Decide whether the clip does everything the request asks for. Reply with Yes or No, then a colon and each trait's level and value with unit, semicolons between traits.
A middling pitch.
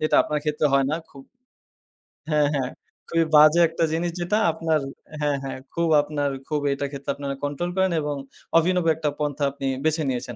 Yes: medium, 150 Hz